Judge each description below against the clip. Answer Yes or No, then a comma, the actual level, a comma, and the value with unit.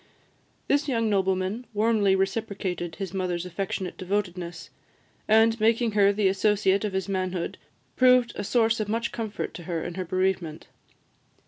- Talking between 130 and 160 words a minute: Yes, average, 145 wpm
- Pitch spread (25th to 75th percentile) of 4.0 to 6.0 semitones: No, average, 3.1 semitones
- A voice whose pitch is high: Yes, high, 195 Hz